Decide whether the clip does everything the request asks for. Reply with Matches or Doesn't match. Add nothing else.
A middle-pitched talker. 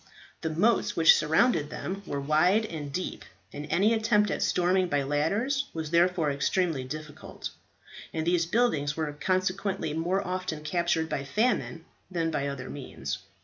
Matches